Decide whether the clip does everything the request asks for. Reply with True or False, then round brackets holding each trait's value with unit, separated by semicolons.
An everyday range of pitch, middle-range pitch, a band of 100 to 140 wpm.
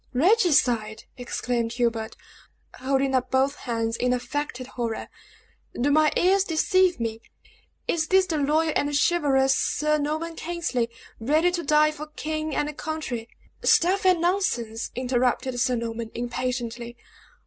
False (4.5 semitones; 270 Hz; 135 wpm)